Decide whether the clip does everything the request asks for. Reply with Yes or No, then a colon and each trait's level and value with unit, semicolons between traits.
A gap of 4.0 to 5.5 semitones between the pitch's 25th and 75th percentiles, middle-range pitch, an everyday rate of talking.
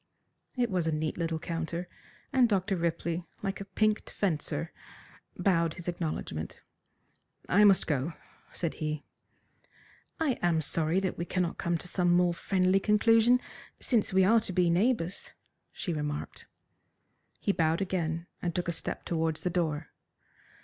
No: average, 3.1 semitones; medium, 175 Hz; average, 150 wpm